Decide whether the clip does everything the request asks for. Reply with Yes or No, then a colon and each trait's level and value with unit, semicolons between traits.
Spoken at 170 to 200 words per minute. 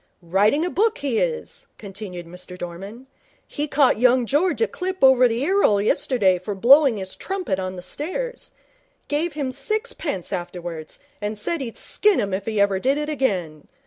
Yes: average, 175 wpm